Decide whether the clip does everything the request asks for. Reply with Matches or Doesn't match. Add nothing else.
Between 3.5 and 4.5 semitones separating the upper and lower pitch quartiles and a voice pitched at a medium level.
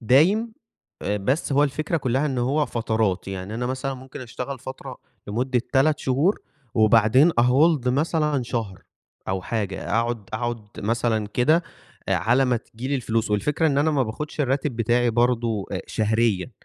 Doesn't match